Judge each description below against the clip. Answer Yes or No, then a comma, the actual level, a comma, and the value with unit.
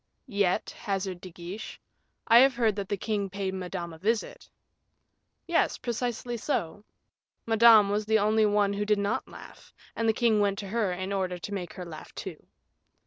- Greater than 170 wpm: Yes, average, 180 wpm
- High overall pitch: Yes, high, 205 Hz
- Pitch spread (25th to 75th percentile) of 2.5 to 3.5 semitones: Yes, average, 2.8 semitones